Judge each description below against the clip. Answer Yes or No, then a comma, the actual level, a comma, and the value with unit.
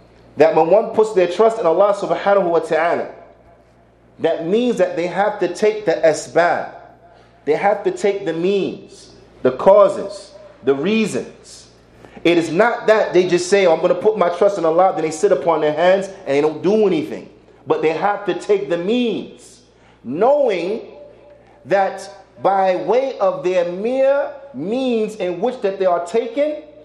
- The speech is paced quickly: No, average, 175 wpm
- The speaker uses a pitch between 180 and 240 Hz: Yes, high, 190 Hz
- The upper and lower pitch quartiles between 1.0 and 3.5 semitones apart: No, average, 4.1 semitones